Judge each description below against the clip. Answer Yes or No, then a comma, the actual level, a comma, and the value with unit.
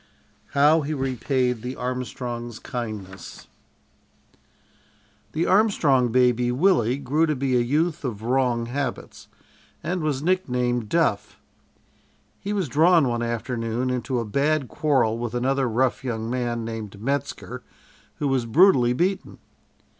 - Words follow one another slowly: Yes, slow, 125 wpm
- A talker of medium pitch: No, low, 125 Hz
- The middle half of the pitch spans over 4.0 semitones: No, average, 3.6 semitones